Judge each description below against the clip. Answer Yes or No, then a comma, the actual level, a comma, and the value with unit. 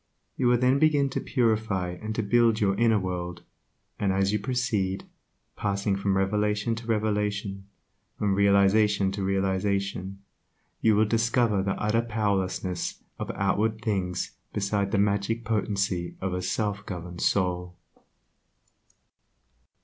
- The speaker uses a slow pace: Yes, slow, 130 wpm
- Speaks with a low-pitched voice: Yes, low, 100 Hz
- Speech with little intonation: Yes, narrow, 2.2 semitones